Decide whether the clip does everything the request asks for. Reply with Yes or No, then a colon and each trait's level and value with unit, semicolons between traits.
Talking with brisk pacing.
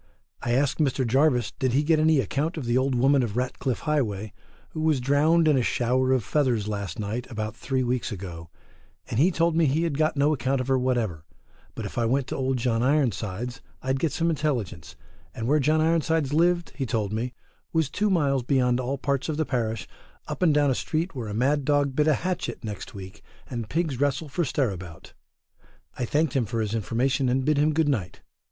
Yes: fast, 210 wpm